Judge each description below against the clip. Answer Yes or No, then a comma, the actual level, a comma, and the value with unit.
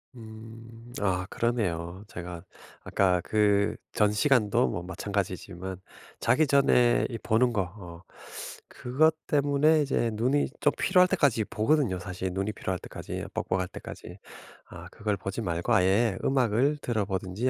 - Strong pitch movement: No, average, 4.7 semitones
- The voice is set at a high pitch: No, low, 105 Hz